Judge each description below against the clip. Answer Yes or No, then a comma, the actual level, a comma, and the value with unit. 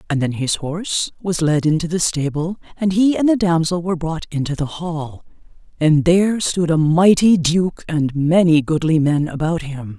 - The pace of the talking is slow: No, average, 185 wpm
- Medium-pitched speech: Yes, medium, 165 Hz